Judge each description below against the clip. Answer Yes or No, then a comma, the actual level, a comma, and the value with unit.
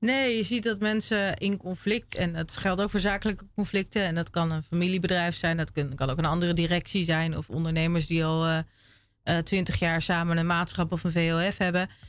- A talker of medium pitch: Yes, medium, 175 Hz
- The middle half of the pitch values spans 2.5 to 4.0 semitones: Yes, average, 3.2 semitones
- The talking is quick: Yes, fast, 220 wpm